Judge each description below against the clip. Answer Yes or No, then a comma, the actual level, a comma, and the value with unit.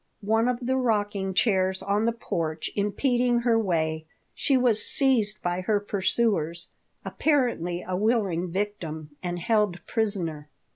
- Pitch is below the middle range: No, high, 205 Hz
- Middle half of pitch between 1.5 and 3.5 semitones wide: No, average, 4.8 semitones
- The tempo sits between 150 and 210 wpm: No, slow, 135 wpm